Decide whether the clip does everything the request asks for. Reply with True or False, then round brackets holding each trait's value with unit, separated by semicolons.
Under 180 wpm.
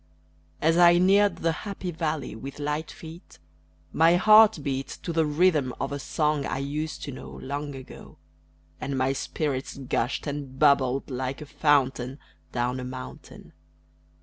True (150 wpm)